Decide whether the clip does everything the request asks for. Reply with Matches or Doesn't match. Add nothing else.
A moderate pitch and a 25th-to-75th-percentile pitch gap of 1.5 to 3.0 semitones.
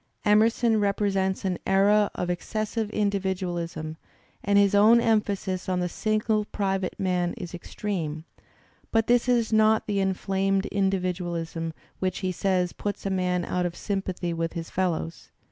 Doesn't match